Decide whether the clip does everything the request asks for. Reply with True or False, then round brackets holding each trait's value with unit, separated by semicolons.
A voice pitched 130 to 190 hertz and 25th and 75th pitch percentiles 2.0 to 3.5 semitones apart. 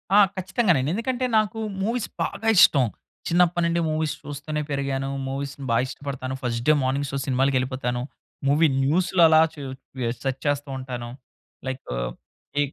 False (140 Hz; 4.3 semitones)